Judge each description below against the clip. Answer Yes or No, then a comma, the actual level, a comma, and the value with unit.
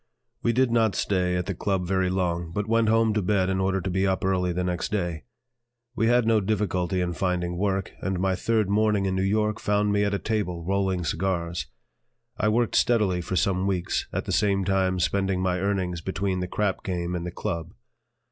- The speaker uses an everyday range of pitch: No, narrow, 2.3 semitones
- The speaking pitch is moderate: No, very low, 95 Hz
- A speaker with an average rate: No, fast, 210 wpm